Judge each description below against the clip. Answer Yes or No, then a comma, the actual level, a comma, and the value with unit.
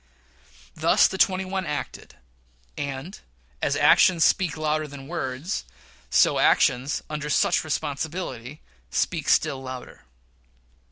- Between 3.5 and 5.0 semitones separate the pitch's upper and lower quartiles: Yes, average, 4.1 semitones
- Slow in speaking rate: Yes, slow, 110 wpm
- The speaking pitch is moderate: Yes, medium, 150 Hz